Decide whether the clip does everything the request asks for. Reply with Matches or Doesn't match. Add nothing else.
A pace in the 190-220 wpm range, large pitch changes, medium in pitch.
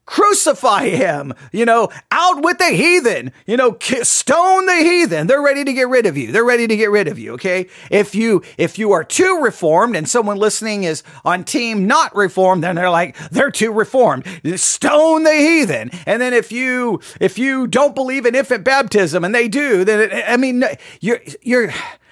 Doesn't match